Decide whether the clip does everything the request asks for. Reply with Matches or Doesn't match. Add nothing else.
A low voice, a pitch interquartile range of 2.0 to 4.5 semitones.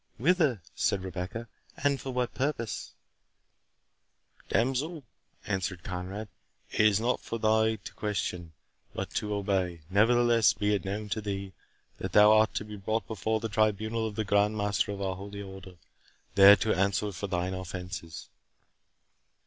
Matches